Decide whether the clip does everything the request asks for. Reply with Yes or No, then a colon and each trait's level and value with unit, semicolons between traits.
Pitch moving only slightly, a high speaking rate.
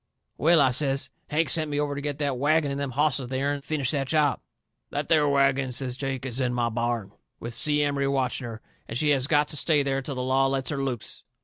Yes: narrow, 2.1 semitones; fast, 245 wpm